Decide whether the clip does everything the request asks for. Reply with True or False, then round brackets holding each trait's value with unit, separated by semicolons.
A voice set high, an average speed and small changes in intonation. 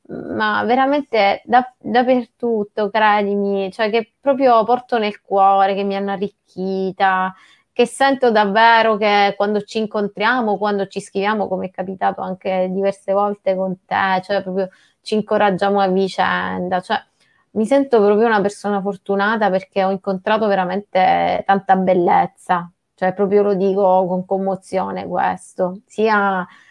True (200 Hz; 135 wpm; 2.2 semitones)